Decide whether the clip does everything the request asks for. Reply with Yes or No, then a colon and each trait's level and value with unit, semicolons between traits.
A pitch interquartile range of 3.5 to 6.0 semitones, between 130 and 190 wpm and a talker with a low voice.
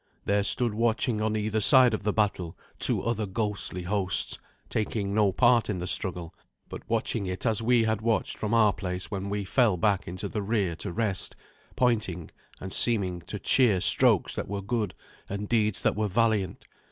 No: average, 2.8 semitones; average, 185 wpm; low, 105 Hz